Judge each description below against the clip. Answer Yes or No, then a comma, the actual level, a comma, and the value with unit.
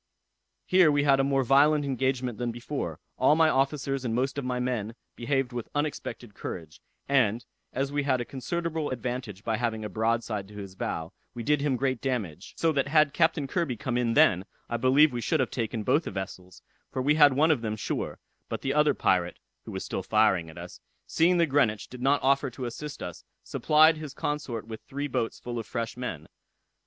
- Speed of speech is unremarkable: No, fast, 210 wpm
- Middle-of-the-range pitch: No, low, 130 Hz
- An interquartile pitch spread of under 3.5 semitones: No, average, 4.1 semitones